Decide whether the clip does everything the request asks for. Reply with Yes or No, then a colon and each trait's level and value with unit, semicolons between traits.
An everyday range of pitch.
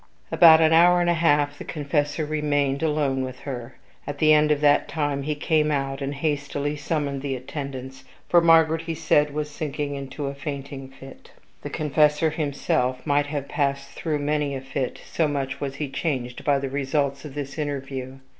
No: narrow, 1.8 semitones